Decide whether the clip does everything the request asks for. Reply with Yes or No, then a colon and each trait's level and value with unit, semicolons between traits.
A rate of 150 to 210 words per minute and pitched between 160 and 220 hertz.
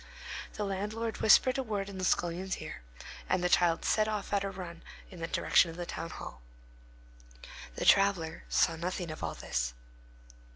Yes: average, 175 wpm; medium, 185 Hz